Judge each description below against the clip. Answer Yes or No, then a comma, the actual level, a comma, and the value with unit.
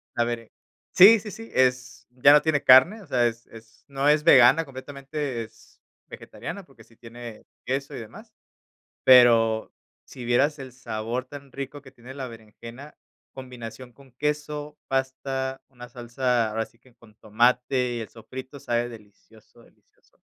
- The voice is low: Yes, low, 125 Hz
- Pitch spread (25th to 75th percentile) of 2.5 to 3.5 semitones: Yes, average, 2.8 semitones